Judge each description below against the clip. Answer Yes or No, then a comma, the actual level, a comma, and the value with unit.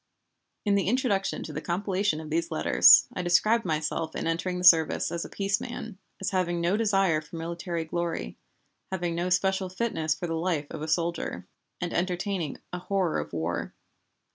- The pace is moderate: Yes, average, 180 wpm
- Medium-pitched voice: Yes, medium, 175 Hz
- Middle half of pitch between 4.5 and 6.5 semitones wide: No, average, 2.8 semitones